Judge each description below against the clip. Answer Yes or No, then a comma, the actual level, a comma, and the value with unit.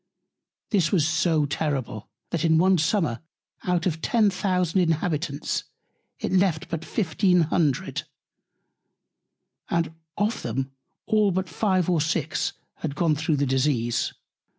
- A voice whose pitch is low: No, medium, 165 Hz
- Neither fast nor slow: No, slow, 130 wpm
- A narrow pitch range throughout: No, average, 3.7 semitones